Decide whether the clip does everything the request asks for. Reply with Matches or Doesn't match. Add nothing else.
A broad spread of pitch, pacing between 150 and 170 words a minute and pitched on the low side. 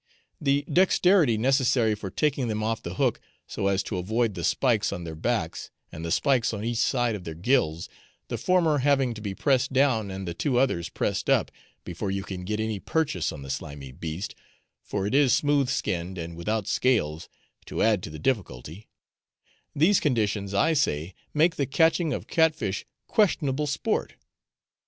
Doesn't match